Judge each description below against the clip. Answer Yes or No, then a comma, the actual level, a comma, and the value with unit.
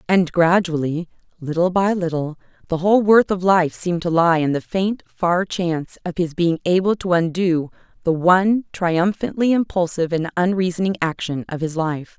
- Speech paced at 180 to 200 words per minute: No, average, 165 wpm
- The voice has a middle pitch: Yes, medium, 175 Hz